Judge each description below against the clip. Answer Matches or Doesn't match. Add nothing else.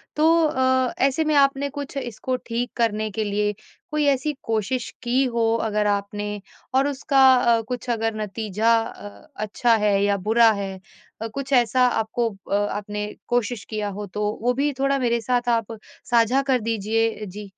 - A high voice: Matches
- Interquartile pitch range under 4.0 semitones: Matches